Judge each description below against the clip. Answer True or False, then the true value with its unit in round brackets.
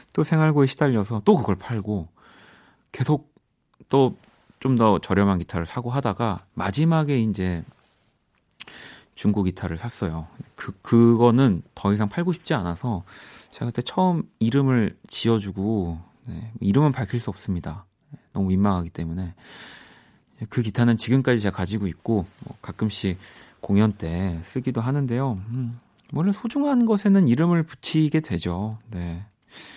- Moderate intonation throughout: False (5.8 semitones)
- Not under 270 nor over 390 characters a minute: True (280 characters per minute)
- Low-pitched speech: True (115 Hz)